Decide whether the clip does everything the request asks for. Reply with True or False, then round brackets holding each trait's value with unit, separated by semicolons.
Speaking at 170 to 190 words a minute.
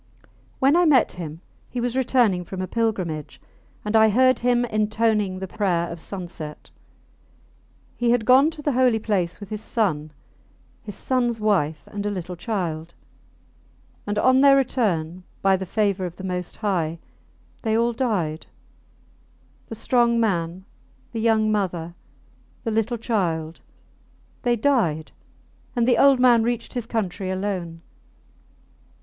False (145 wpm)